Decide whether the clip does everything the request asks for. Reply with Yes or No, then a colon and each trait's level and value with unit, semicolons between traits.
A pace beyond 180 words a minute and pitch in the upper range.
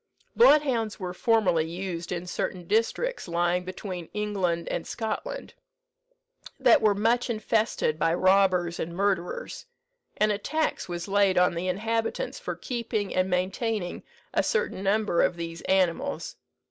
No: slow, 135 wpm; high, 195 Hz